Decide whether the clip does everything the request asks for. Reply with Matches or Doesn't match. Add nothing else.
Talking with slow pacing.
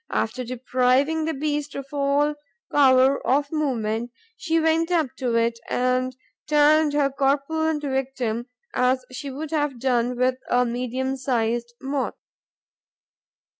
Matches